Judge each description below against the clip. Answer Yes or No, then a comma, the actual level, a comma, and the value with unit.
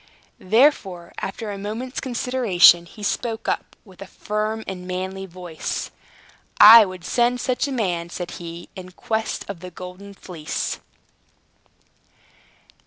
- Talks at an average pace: No, slow, 130 wpm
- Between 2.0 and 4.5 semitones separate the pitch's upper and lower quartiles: Yes, average, 3.6 semitones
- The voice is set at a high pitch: Yes, high, 195 Hz